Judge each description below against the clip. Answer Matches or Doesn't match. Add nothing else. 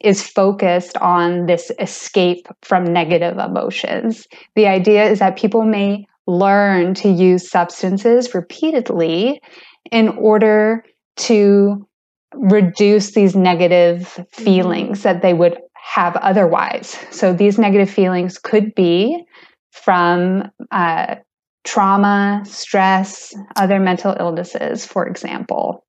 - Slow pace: Matches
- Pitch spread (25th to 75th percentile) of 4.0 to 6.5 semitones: Doesn't match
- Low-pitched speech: Doesn't match